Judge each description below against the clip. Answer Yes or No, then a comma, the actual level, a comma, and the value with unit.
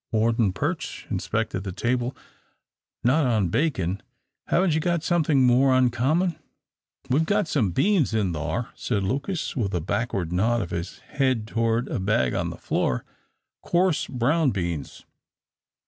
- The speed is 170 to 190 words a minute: No, average, 145 wpm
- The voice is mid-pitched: No, low, 120 Hz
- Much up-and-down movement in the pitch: Yes, wide, 7.2 semitones